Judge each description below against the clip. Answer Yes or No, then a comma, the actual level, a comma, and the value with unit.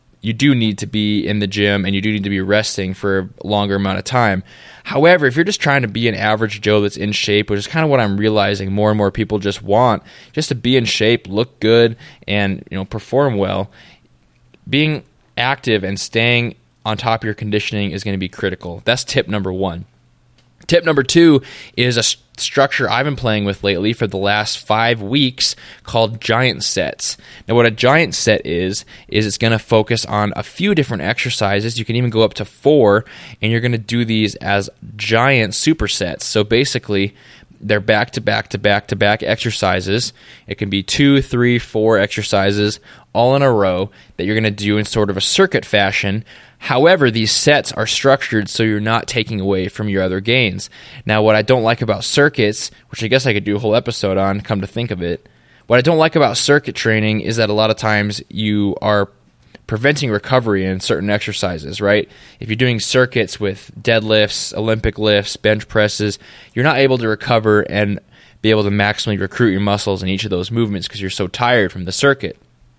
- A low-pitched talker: Yes, low, 110 Hz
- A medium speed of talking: No, fast, 210 wpm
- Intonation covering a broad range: No, average, 3.0 semitones